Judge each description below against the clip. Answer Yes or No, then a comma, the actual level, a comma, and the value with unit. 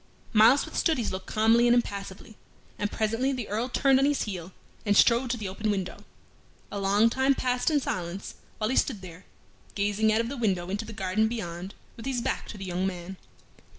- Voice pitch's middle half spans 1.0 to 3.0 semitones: No, average, 3.8 semitones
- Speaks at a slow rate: No, fast, 205 wpm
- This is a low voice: No, high, 215 Hz